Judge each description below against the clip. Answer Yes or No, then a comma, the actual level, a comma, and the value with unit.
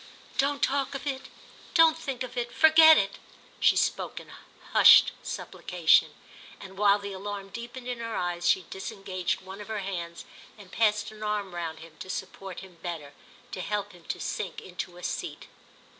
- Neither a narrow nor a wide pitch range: Yes, average, 4.5 semitones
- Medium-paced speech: Yes, average, 175 wpm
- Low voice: No, high, 200 Hz